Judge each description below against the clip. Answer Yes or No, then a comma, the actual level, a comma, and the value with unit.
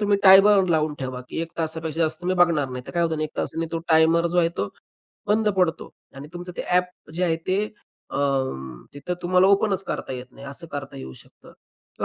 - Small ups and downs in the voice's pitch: No, average, 3.0 semitones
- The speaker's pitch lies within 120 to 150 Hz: No, medium, 165 Hz